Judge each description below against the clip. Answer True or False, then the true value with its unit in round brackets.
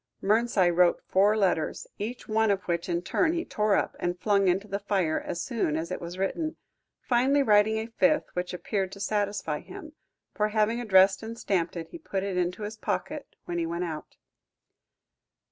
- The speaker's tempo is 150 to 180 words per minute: False (190 wpm)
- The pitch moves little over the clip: False (3.7 semitones)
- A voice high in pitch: True (200 Hz)